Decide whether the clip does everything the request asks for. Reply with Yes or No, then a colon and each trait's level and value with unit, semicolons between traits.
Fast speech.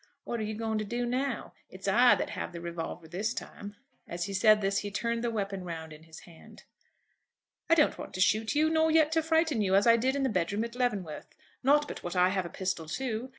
Yes: fast, 245 wpm